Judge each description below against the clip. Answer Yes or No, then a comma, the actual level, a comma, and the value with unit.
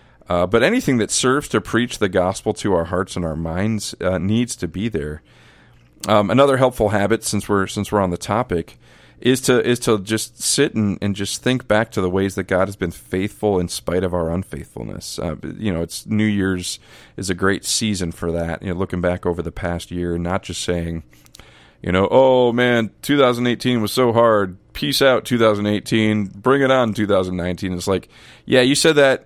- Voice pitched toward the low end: Yes, low, 105 Hz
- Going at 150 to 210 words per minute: Yes, fast, 205 wpm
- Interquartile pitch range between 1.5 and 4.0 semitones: No, average, 4.6 semitones